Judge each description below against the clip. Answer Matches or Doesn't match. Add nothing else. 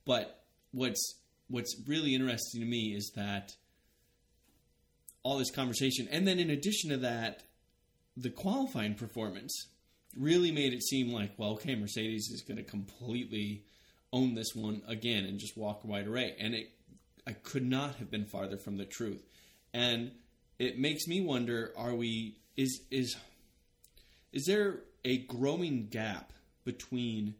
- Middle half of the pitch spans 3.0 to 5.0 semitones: Matches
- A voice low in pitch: Matches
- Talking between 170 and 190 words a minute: Doesn't match